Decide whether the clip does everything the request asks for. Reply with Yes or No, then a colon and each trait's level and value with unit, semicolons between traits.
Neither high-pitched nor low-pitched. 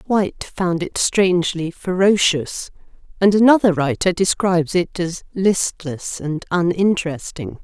Yes: medium, 180 Hz